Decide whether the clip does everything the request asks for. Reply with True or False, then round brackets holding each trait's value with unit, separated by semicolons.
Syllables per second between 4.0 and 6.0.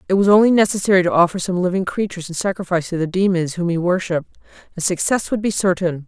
False (7.0 syllables/s)